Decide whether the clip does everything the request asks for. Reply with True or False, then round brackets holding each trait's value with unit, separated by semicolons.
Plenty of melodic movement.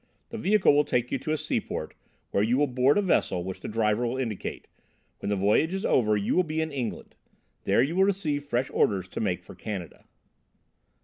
True (6.6 semitones)